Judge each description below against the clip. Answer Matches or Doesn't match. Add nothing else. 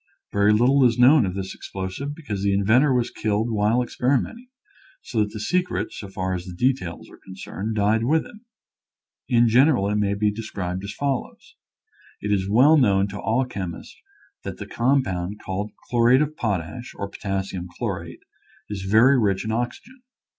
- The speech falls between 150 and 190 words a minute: Matches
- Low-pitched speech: Matches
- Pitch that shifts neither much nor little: Matches